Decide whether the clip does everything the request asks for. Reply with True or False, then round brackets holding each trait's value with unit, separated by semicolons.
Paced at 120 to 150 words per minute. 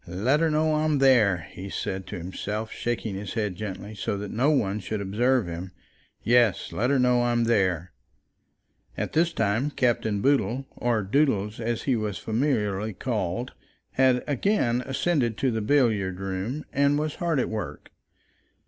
False (160 wpm)